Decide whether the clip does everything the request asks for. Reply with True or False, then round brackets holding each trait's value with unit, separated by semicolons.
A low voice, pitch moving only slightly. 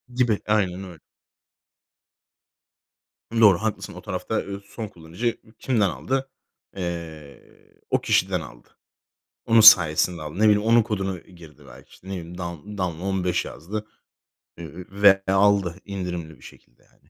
False (95 Hz; 3.5 semitones)